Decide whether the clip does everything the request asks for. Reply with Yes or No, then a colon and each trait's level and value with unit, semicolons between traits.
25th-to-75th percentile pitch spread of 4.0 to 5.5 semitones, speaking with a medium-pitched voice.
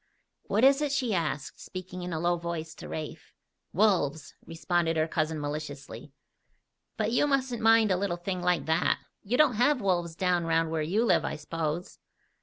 Yes: average, 5.1 semitones; medium, 175 Hz